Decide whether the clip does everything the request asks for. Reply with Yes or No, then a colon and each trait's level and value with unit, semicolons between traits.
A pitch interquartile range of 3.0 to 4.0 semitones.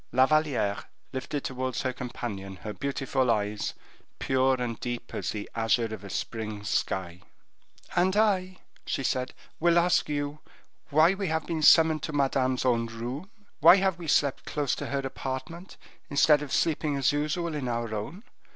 No: average, 5.0 semitones